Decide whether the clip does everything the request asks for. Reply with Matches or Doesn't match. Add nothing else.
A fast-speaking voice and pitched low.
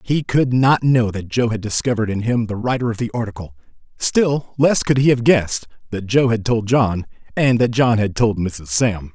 Matches